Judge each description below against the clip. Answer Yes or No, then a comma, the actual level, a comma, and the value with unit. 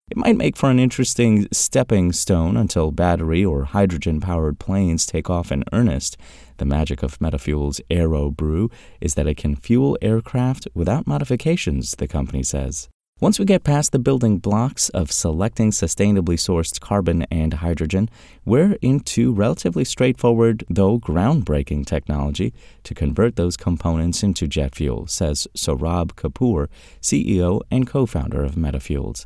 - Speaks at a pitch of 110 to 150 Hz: No, very low, 85 Hz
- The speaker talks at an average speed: Yes, average, 145 wpm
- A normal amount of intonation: No, wide, 7.1 semitones